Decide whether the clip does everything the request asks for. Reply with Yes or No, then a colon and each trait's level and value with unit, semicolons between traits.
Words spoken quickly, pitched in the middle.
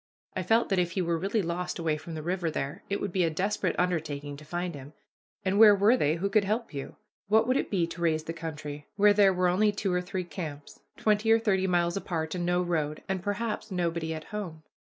Yes: fast, 235 wpm; medium, 180 Hz